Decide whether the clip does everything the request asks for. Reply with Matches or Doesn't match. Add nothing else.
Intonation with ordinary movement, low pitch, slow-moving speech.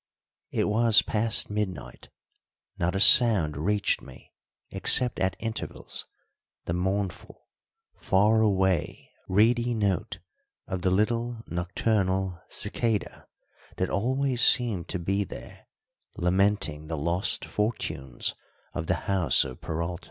Matches